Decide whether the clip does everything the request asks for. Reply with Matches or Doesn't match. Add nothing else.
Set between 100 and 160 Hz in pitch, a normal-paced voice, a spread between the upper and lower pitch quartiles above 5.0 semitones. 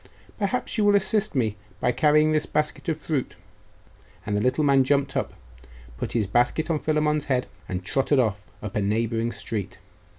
Matches